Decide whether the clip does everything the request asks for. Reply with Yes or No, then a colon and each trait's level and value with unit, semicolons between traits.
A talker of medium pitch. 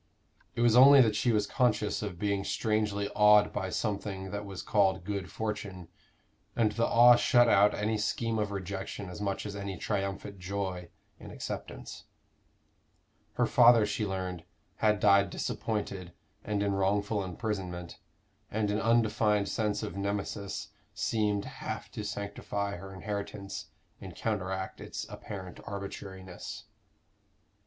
No: low, 100 Hz